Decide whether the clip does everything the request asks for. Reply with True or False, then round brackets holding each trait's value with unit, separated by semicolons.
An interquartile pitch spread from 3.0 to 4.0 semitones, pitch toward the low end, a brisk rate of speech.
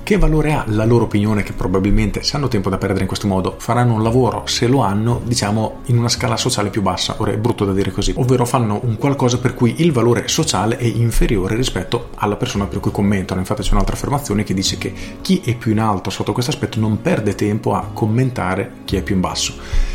True (3.5 semitones; 110 Hz; 230 wpm)